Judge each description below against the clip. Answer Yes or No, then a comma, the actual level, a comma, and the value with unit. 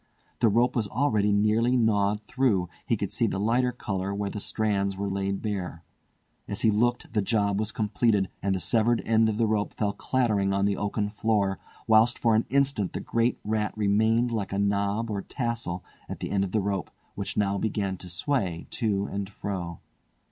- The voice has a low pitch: Yes, low, 105 Hz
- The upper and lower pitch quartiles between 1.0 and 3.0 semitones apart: Yes, narrow, 2.4 semitones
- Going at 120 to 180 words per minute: No, average, 190 wpm